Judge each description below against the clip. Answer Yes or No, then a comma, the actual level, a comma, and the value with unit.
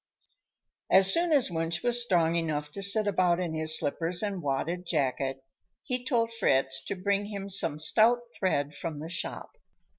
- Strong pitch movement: No, average, 4.6 semitones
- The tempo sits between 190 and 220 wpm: No, average, 170 wpm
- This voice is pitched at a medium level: Yes, medium, 175 Hz